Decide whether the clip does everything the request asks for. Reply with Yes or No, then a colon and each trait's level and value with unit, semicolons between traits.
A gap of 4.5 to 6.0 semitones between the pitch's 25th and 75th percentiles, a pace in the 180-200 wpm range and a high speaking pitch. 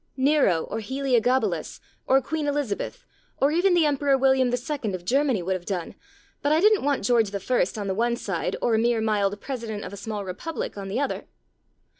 Yes: wide, 5.6 semitones; average, 195 wpm; high, 245 Hz